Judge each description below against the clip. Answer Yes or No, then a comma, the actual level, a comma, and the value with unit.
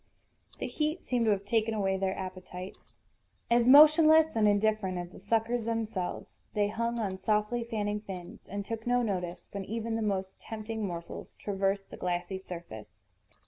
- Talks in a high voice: Yes, high, 210 Hz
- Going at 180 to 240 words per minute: No, average, 165 wpm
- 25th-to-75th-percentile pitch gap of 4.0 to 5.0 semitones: No, average, 3.2 semitones